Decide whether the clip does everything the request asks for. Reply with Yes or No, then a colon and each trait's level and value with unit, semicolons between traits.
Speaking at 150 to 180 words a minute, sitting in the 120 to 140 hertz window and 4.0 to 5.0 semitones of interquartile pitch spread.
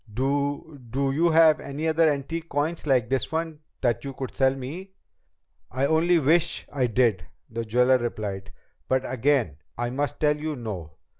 Yes: average, 165 wpm; low, 135 Hz; average, 4.4 semitones